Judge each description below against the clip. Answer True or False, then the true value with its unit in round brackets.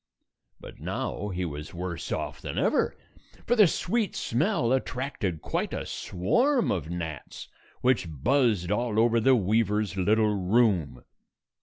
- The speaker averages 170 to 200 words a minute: False (135 wpm)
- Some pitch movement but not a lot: False (6.0 semitones)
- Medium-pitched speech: False (105 Hz)